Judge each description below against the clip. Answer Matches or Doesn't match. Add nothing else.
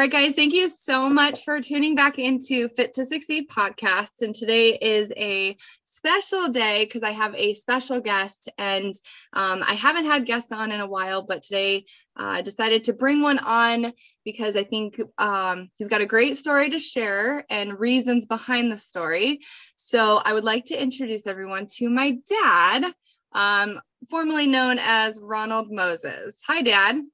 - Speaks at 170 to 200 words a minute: Matches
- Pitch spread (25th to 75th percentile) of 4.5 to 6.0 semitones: Matches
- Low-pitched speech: Doesn't match